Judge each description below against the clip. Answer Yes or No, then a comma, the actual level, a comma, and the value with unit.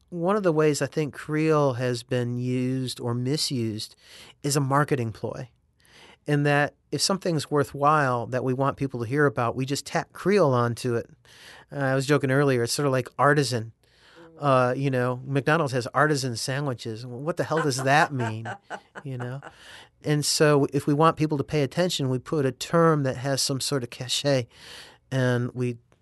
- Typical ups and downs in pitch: Yes, average, 3.0 semitones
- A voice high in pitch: No, low, 135 Hz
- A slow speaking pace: No, average, 185 wpm